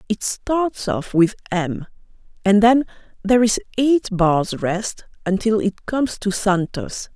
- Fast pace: No, average, 145 wpm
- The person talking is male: No, female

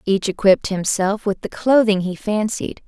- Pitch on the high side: Yes, high, 205 Hz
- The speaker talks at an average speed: Yes, average, 165 wpm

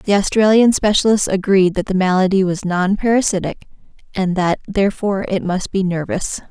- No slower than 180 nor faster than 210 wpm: No, average, 155 wpm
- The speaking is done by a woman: Yes, female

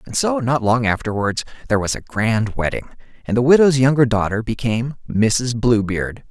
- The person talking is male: Yes, male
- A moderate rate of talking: Yes, average, 170 wpm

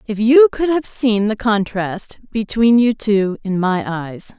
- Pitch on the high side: Yes, high, 220 Hz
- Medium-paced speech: Yes, average, 180 wpm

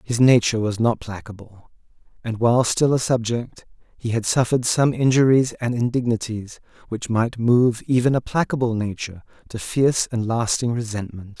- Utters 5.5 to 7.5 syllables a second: No, 5.2 syllables/s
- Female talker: No, male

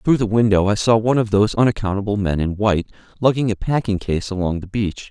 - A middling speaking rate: No, fast, 225 wpm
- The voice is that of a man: Yes, male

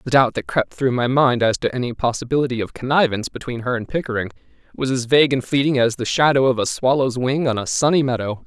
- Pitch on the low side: Yes, low, 125 Hz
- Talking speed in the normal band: No, fast, 235 wpm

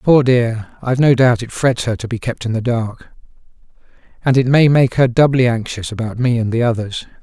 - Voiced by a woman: No, male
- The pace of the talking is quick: Yes, fast, 215 wpm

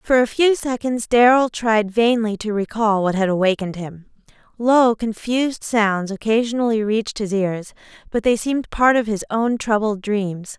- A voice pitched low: No, high, 220 Hz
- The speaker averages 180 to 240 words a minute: No, average, 165 wpm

